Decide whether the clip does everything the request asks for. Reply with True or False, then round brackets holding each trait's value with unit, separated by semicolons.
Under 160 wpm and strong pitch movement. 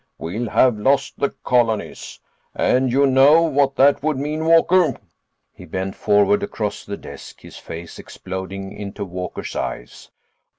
True (140 wpm; 6.3 semitones)